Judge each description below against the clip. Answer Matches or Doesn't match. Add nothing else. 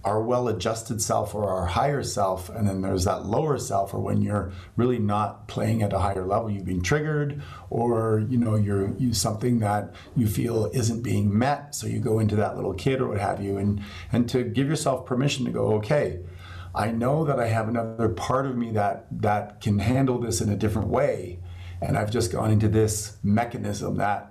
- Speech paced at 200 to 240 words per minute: Matches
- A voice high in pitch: Doesn't match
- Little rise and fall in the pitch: Doesn't match